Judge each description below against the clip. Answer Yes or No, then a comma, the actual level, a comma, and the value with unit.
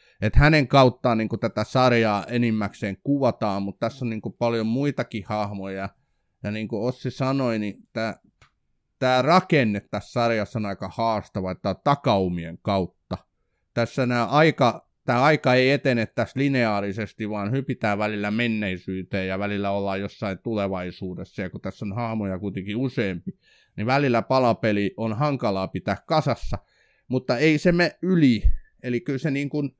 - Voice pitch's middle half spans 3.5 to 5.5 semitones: Yes, average, 4.5 semitones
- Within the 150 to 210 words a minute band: Yes, fast, 155 wpm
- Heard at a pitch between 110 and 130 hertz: Yes, low, 115 Hz